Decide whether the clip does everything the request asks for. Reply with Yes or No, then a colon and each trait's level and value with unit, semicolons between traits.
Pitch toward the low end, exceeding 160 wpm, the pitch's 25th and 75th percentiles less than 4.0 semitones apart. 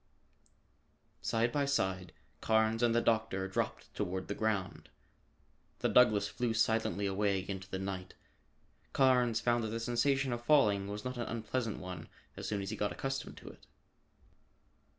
No: low, 110 Hz; average, 155 wpm; average, 3.5 semitones